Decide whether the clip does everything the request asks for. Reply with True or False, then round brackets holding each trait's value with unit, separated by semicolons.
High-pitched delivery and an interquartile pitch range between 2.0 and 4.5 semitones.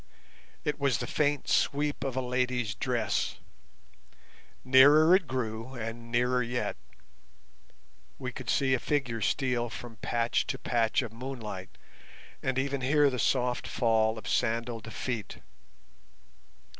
False (125 Hz; 2.6 semitones)